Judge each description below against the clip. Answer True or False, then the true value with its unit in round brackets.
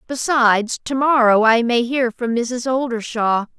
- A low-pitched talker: False (240 Hz)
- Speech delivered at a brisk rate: False (150 wpm)